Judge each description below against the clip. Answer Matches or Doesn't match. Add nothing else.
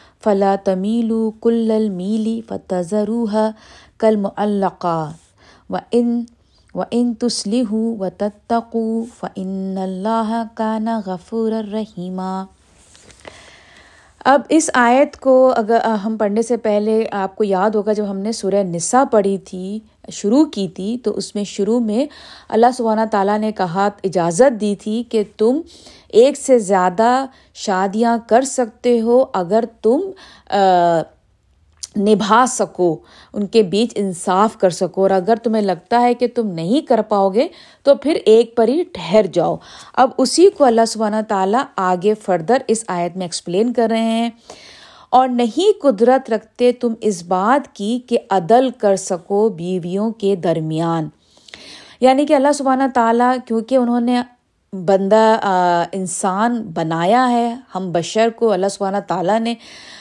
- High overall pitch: Matches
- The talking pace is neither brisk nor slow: Matches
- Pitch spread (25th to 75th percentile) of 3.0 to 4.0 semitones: Matches